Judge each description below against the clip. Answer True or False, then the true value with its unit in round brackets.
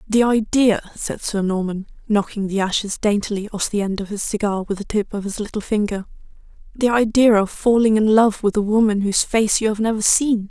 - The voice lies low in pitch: False (210 Hz)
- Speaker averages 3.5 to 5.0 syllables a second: False (5.5 syllables/s)